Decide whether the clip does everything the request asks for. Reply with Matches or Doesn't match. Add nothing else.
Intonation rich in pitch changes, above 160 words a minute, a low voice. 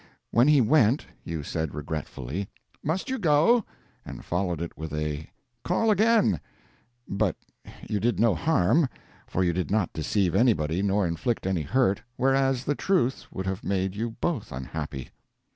Doesn't match